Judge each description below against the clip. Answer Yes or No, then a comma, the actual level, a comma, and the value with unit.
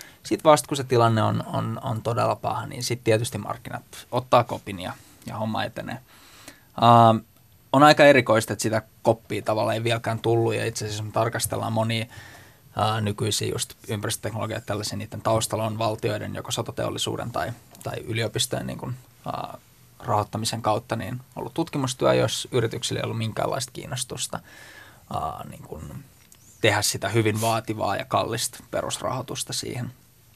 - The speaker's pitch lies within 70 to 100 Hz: No, low, 115 Hz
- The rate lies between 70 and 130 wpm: No, average, 145 wpm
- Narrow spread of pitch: Yes, narrow, 2.3 semitones